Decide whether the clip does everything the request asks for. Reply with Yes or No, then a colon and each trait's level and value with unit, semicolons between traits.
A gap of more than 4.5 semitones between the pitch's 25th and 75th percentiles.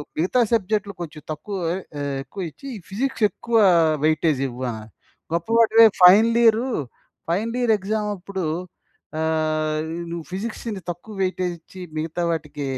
Yes: wide, 5.6 semitones